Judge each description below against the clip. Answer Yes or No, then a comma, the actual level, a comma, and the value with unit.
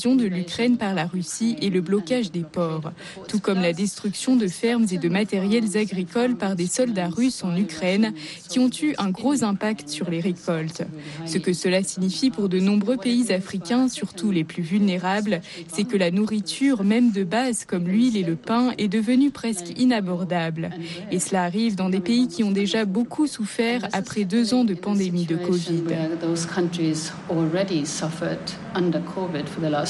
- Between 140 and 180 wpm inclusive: Yes, average, 165 wpm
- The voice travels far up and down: No, average, 4.3 semitones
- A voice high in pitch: Yes, high, 195 Hz